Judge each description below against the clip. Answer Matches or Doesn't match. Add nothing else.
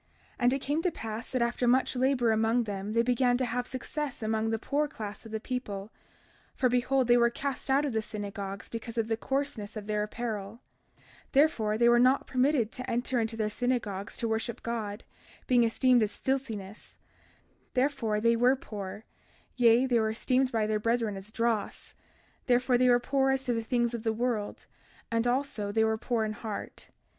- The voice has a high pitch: Matches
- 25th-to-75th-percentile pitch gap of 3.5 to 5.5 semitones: Doesn't match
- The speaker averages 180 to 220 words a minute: Matches